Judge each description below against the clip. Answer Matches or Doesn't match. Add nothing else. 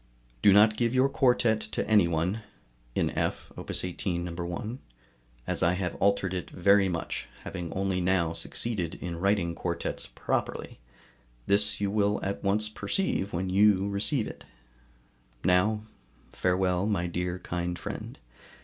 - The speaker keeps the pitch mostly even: Doesn't match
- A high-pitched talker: Doesn't match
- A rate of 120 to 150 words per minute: Matches